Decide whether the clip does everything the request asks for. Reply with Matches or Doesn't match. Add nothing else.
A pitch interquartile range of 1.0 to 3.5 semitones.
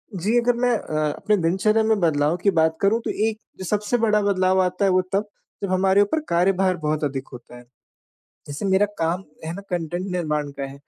Doesn't match